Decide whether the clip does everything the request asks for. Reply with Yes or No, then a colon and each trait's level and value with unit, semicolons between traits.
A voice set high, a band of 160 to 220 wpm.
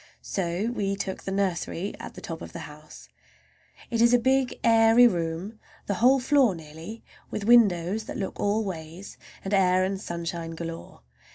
Yes: high, 195 Hz; average, 170 wpm